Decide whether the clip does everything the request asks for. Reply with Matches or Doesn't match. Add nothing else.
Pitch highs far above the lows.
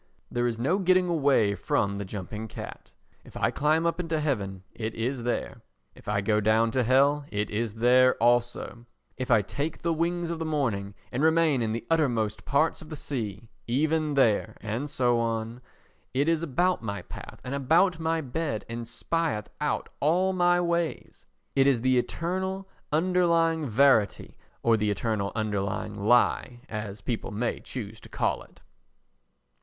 Matches